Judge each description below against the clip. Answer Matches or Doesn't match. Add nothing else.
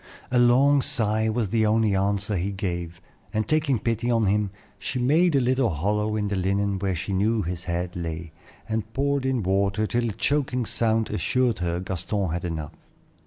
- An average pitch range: Matches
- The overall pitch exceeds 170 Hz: Doesn't match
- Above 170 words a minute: Matches